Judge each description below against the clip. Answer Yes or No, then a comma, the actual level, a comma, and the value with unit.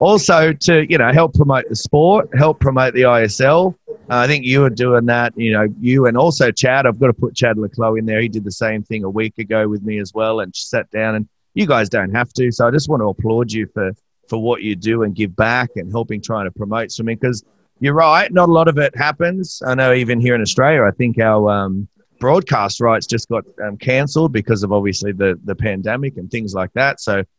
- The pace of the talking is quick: Yes, fast, 245 wpm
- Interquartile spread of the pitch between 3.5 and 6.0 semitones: Yes, average, 4.0 semitones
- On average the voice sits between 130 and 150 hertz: No, low, 115 Hz